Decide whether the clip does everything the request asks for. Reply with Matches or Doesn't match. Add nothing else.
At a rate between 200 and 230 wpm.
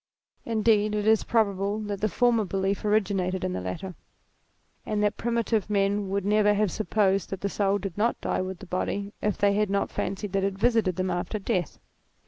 Matches